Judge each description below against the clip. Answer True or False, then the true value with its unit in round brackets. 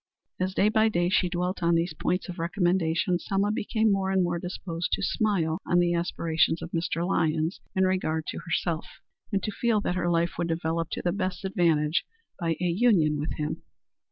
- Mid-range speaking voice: True (175 Hz)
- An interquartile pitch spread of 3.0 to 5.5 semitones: False (2.4 semitones)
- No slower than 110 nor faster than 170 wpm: False (195 wpm)